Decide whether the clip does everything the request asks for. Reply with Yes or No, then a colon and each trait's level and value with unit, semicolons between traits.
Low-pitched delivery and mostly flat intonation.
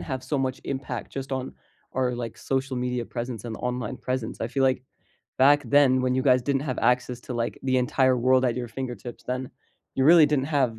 Yes: low, 130 Hz; narrow, 1.3 semitones